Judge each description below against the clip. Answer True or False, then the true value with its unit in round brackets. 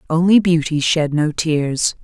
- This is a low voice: False (160 Hz)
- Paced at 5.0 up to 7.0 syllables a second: False (3.9 syllables/s)